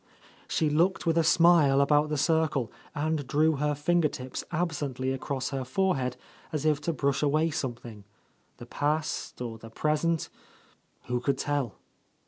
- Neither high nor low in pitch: Yes, medium, 145 Hz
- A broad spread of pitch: No, average, 3.1 semitones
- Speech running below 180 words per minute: Yes, average, 155 wpm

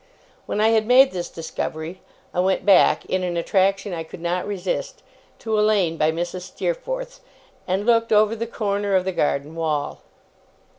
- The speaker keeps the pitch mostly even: No, average, 3.9 semitones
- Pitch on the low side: No, high, 190 Hz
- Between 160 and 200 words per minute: Yes, average, 170 wpm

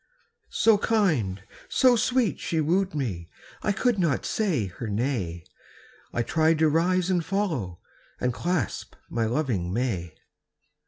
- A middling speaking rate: No, slow, 130 wpm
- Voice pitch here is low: No, medium, 155 Hz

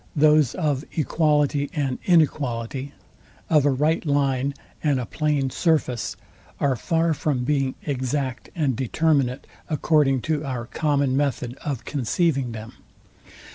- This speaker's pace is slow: Yes, slow, 125 wpm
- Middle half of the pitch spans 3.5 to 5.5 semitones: No, average, 2.7 semitones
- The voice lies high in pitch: No, medium, 140 Hz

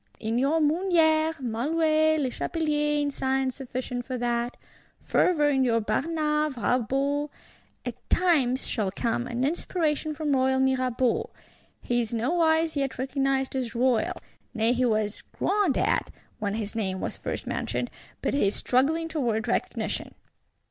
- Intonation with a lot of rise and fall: No, average, 4.2 semitones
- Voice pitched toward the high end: Yes, very high, 265 Hz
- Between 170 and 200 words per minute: No, average, 140 wpm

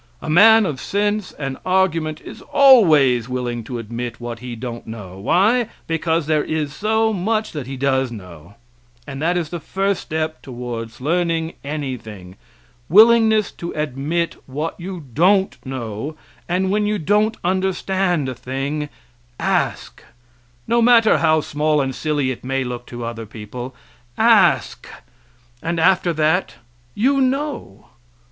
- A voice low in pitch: No, medium, 155 Hz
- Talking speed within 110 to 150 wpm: Yes, average, 140 wpm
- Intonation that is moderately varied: No, wide, 7.0 semitones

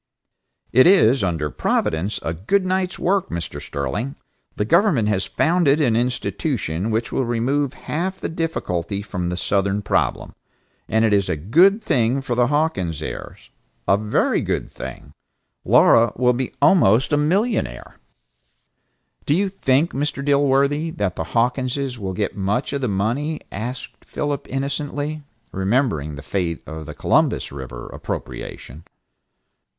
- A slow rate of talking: No, average, 145 wpm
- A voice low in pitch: Yes, low, 120 Hz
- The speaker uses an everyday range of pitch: No, wide, 7.2 semitones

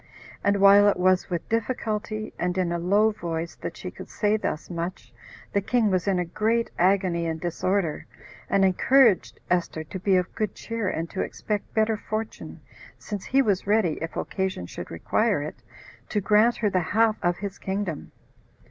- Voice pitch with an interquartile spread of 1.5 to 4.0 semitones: Yes, average, 3.4 semitones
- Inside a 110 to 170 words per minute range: No, average, 180 wpm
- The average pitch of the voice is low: No, high, 195 Hz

